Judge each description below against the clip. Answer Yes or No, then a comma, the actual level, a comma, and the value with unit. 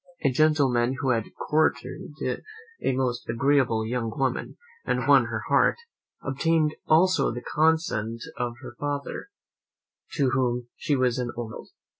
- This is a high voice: No, low, 130 Hz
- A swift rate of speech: No, average, 140 wpm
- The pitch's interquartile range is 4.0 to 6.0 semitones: No, average, 3.5 semitones